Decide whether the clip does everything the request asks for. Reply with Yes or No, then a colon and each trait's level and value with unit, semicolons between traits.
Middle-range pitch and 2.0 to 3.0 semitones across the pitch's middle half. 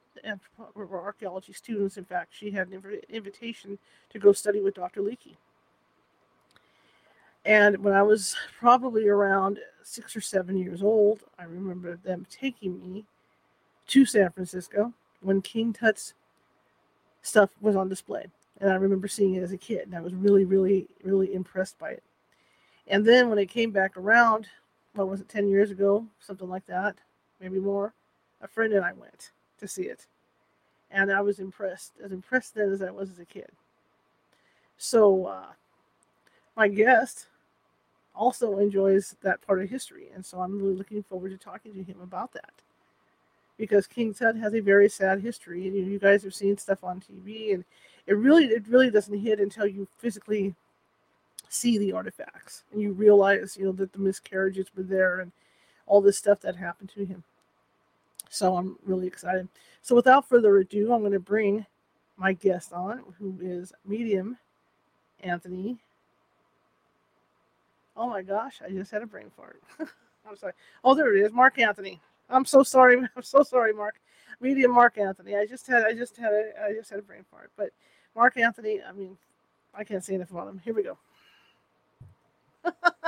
No: high, 200 Hz; narrow, 2.6 semitones